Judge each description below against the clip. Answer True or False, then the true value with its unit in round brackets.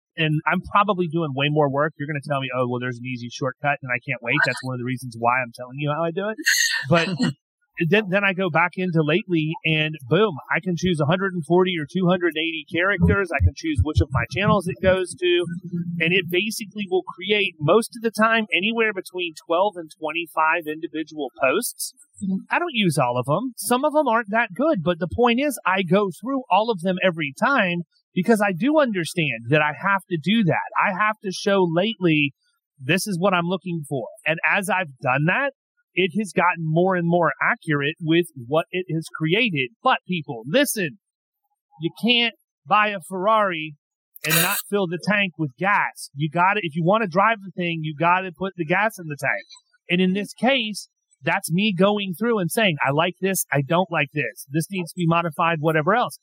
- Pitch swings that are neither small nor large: True (4.5 semitones)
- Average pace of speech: False (210 wpm)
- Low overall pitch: False (180 Hz)